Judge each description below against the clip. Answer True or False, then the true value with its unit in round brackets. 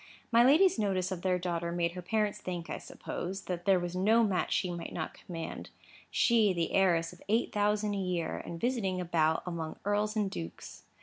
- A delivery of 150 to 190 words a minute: False (200 wpm)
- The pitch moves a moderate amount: True (3.4 semitones)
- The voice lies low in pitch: False (185 Hz)